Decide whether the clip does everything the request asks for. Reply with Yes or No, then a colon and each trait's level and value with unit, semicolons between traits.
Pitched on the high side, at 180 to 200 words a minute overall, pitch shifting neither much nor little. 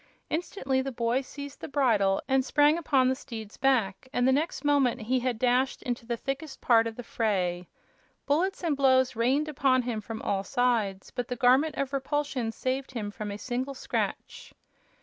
Yes: very high, 255 Hz; average, 185 wpm; average, 3.2 semitones